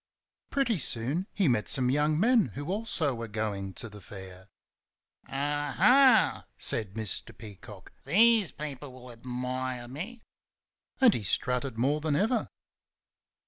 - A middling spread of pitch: No, wide, 8.1 semitones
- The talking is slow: Yes, slow, 130 wpm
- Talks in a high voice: No, low, 135 Hz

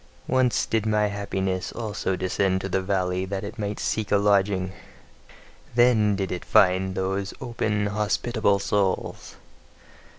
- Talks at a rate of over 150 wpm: No, slow, 135 wpm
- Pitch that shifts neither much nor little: No, narrow, 2.0 semitones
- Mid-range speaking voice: No, low, 100 Hz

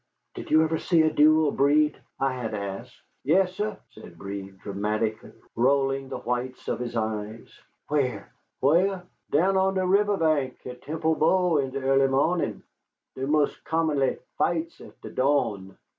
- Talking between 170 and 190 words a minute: No, average, 155 wpm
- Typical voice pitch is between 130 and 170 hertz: Yes, medium, 140 Hz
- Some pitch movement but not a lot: Yes, average, 4.8 semitones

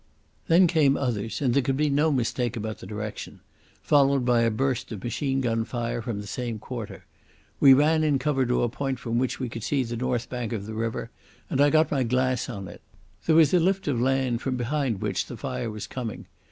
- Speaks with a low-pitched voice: Yes, low, 125 Hz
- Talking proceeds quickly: Yes, fast, 220 wpm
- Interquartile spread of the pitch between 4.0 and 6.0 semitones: No, average, 3.3 semitones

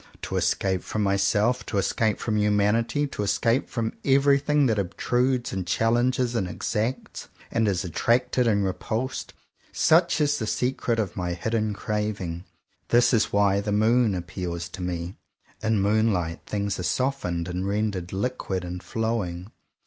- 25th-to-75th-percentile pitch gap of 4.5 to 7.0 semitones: No, average, 4.1 semitones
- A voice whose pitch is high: No, low, 105 Hz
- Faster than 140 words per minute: Yes, average, 160 wpm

